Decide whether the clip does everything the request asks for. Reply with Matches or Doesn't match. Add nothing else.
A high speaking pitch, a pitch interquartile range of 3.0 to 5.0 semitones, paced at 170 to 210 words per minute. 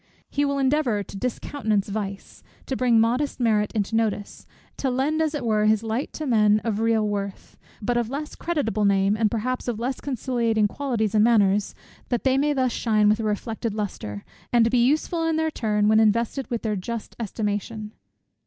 Matches